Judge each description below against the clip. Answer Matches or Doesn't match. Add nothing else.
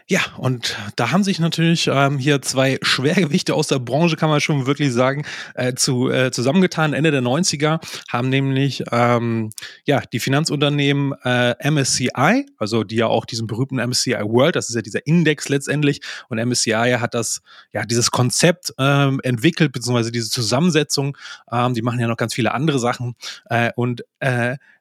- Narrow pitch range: Doesn't match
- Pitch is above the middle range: Doesn't match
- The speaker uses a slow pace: Doesn't match